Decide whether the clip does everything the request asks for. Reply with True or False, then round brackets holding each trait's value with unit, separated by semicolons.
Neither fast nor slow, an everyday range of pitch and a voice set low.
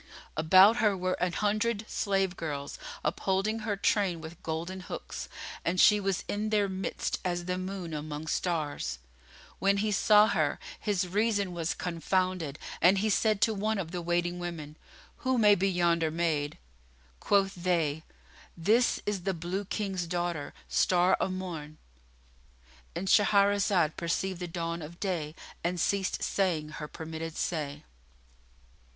False (145 wpm; 3.6 semitones; 180 Hz)